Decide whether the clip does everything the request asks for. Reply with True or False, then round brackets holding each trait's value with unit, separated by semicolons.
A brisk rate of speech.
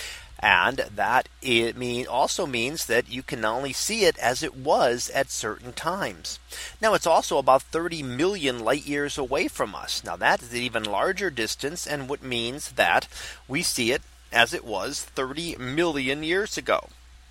False (175 wpm)